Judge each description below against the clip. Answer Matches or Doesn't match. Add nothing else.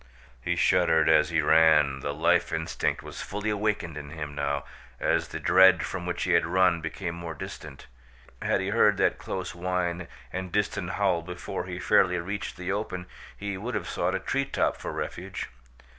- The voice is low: Matches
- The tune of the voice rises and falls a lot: Doesn't match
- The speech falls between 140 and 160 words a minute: Doesn't match